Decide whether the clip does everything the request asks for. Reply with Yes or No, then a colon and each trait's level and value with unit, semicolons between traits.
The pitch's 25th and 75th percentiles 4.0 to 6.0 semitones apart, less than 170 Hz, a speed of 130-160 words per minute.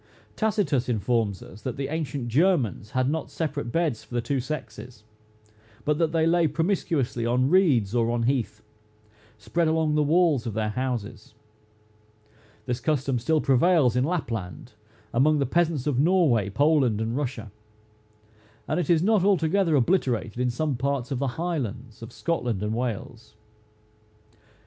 Yes: average, 5.3 semitones; low, 135 Hz; average, 150 wpm